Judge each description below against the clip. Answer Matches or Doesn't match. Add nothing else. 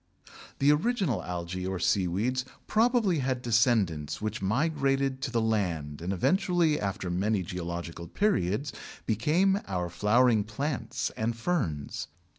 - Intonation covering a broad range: Matches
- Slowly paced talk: Matches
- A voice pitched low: Matches